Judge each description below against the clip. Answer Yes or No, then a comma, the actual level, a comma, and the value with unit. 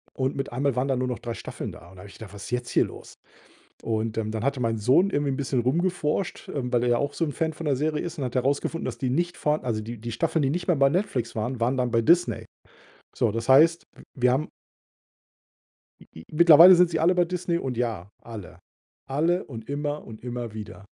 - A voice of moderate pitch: No, low, 130 Hz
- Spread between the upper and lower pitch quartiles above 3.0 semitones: Yes, average, 5.1 semitones